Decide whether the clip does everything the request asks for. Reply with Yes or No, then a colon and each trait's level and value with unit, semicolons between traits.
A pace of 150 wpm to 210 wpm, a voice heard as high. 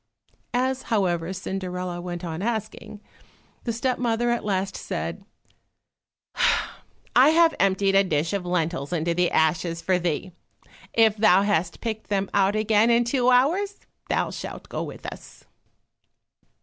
No: average, 140 wpm; high, 195 Hz